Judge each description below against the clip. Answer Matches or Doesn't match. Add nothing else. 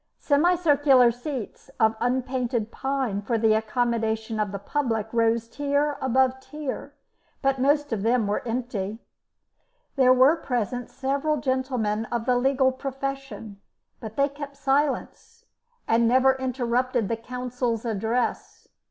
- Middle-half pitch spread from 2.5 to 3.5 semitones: Matches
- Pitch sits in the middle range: Doesn't match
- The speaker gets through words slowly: Matches